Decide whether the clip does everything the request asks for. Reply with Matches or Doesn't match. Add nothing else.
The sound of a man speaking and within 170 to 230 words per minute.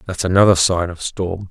Matches